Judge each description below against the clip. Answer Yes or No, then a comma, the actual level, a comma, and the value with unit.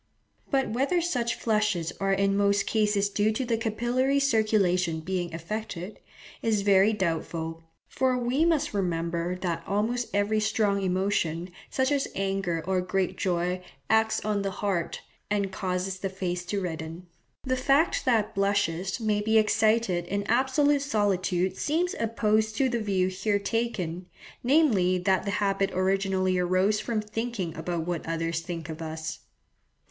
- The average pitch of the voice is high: Yes, high, 200 Hz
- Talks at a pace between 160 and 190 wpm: No, average, 150 wpm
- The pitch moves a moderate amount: Yes, average, 3.5 semitones